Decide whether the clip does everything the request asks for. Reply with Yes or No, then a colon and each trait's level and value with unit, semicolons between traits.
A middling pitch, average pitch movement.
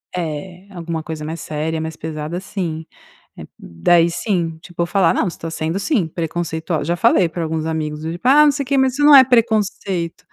Yes: medium, 170 Hz; average, 3.4 semitones